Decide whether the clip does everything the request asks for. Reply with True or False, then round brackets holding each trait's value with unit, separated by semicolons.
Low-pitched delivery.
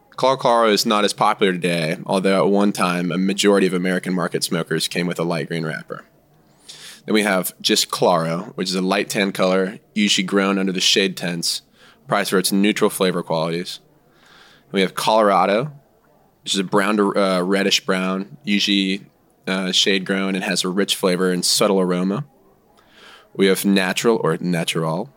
True (95 Hz)